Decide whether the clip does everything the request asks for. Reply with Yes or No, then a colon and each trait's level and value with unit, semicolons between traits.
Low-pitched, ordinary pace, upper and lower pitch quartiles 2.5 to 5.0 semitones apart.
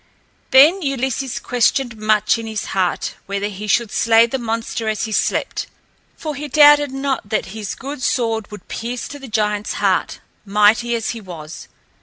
No: high, 230 Hz; average, 170 wpm; average, 4.1 semitones